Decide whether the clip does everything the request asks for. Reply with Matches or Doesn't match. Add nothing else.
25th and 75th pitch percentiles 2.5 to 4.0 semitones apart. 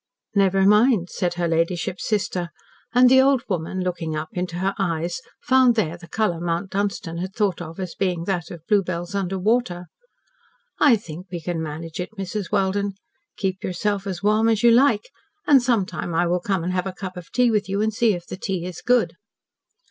Matches